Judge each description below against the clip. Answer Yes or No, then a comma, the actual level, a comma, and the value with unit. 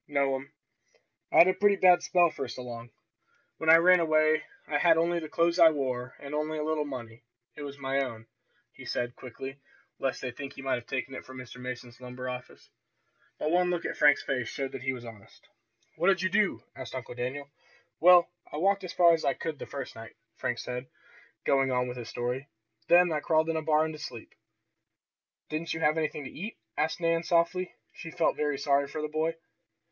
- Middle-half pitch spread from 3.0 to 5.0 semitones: Yes, average, 4.4 semitones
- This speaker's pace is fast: Yes, fast, 210 wpm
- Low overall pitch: No, medium, 145 Hz